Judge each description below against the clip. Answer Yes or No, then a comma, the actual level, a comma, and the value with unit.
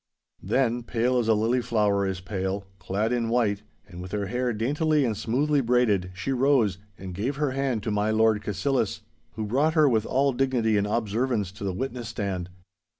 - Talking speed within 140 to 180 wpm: No, average, 190 wpm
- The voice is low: Yes, low, 115 Hz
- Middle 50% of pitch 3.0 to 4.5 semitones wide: Yes, average, 3.9 semitones